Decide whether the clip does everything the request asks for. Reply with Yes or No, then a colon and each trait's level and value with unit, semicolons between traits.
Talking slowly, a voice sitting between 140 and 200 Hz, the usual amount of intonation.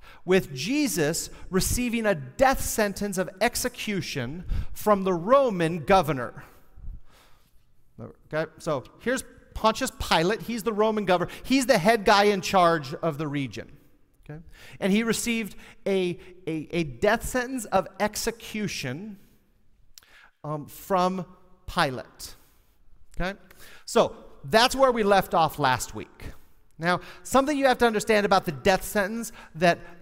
No: slow, 130 wpm; high, 190 Hz; wide, 5.9 semitones